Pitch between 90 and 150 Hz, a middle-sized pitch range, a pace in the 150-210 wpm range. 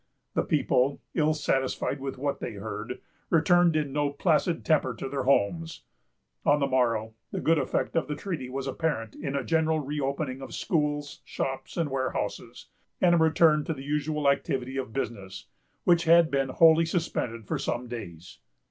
Yes: medium, 140 Hz; average, 3.5 semitones; average, 170 wpm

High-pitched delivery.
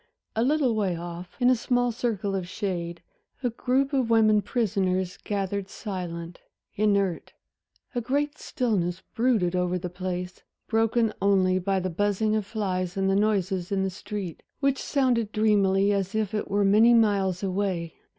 Yes: high, 200 Hz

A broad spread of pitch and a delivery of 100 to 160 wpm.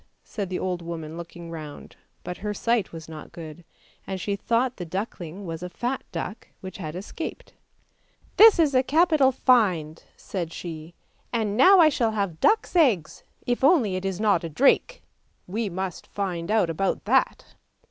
No: wide, 6.1 semitones; average, 175 wpm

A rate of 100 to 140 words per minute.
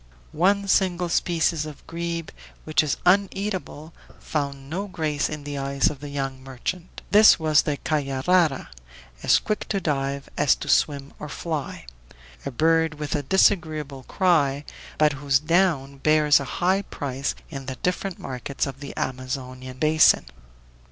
No: average, 150 wpm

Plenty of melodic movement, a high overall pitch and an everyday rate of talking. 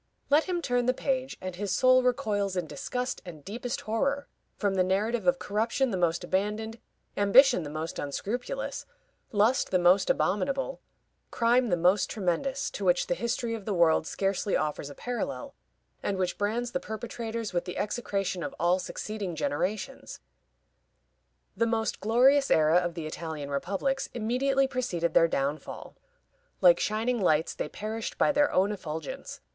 Yes: wide, 5.7 semitones; high, 210 Hz; average, 160 wpm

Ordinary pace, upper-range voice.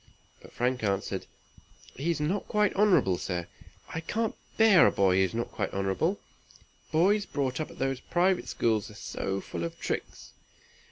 No: average, 170 wpm; low, 135 Hz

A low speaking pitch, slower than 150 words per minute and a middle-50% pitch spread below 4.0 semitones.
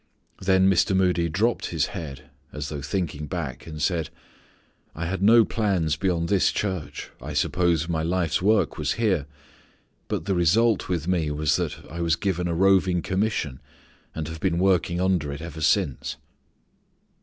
No: very low, 85 Hz; average, 165 wpm; average, 3.2 semitones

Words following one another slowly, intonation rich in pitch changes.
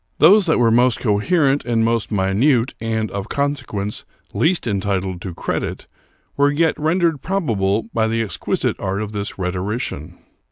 No: average, 150 wpm; wide, 6.2 semitones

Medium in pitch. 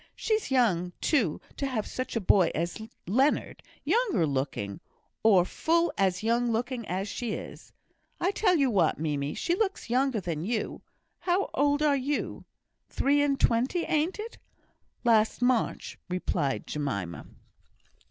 No: high, 235 Hz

